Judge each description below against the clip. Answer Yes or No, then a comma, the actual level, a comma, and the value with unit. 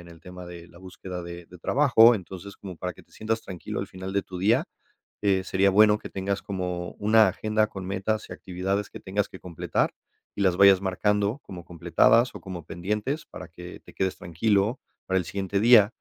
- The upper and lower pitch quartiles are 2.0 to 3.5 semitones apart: Yes, narrow, 2.5 semitones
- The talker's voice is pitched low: Yes, very low, 95 Hz